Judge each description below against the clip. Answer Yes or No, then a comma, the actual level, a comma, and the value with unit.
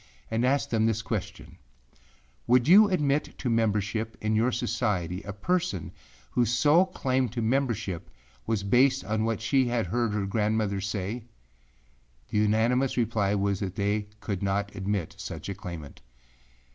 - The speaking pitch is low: Yes, low, 110 Hz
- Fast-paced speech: No, average, 150 wpm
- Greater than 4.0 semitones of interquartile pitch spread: No, average, 3.5 semitones